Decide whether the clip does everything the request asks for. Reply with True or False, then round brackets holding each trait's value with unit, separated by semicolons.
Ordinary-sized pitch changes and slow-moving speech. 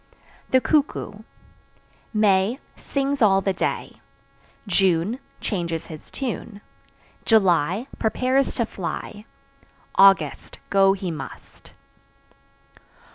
True (4.1 semitones; 85 wpm)